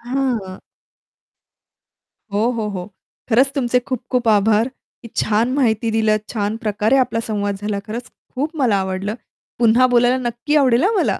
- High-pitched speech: Yes, high, 230 Hz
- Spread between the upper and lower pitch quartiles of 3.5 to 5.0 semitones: No, average, 3.1 semitones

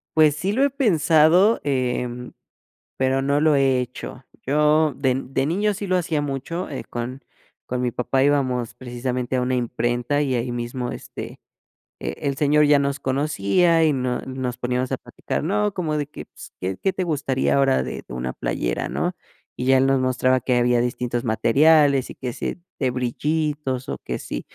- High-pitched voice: No, low, 135 Hz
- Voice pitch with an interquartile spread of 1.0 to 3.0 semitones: No, average, 3.4 semitones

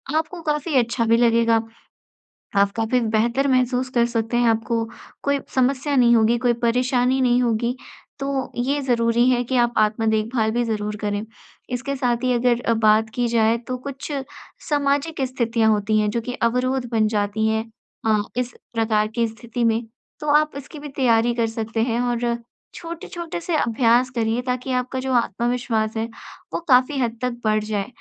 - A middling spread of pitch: No, narrow, 2.3 semitones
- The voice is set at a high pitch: Yes, high, 240 Hz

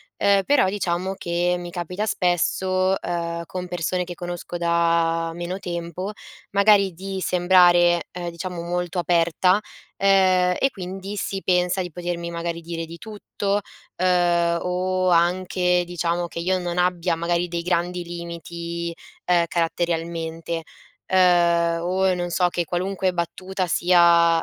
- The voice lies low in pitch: No, medium, 175 Hz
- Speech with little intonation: Yes, narrow, 1.5 semitones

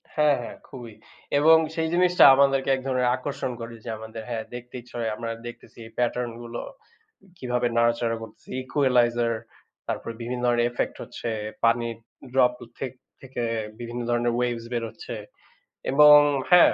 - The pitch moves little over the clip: Yes, narrow, 2.1 semitones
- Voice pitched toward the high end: No, low, 120 Hz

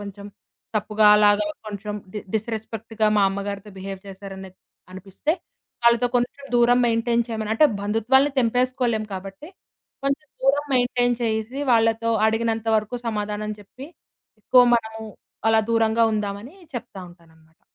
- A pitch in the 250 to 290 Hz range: No, high, 220 Hz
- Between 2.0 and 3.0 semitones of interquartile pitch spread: Yes, average, 2.7 semitones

